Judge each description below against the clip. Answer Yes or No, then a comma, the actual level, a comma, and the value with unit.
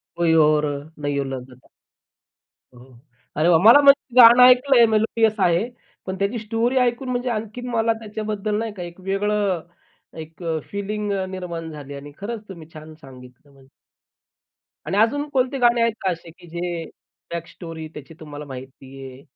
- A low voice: No, high, 190 Hz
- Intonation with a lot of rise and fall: Yes, wide, 6.5 semitones